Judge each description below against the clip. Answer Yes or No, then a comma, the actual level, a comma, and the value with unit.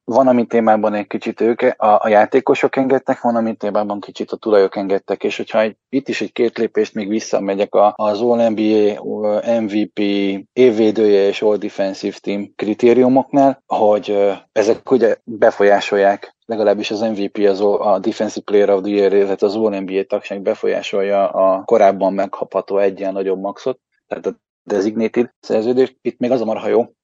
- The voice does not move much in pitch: Yes, narrow, 2.2 semitones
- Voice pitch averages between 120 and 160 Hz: No, low, 105 Hz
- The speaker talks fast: Yes, fast, 160 wpm